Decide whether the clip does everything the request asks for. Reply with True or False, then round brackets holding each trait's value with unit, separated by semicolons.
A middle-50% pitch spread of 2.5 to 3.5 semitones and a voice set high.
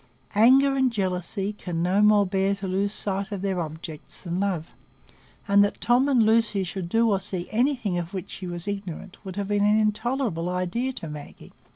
True (3.1 semitones; 200 Hz)